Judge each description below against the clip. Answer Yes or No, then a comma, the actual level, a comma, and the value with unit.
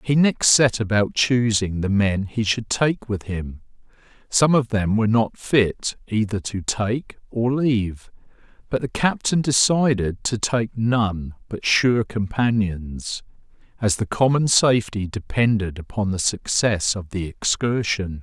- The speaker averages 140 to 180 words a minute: Yes, average, 145 wpm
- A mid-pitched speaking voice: No, low, 110 Hz